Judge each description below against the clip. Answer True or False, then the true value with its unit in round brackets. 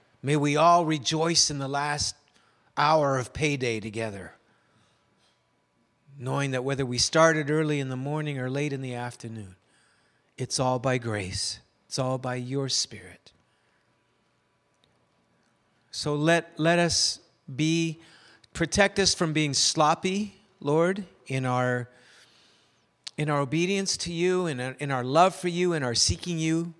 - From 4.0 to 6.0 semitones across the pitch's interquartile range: True (4.5 semitones)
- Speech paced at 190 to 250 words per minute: False (140 wpm)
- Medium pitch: True (145 Hz)